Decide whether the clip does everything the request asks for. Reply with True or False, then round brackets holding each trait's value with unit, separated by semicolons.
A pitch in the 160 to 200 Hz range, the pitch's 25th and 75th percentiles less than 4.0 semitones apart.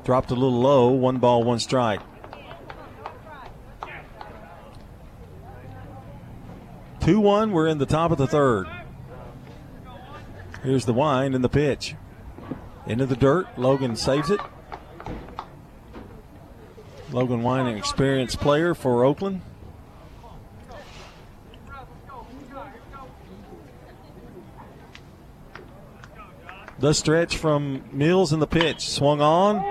False (135 Hz; 3.6 semitones)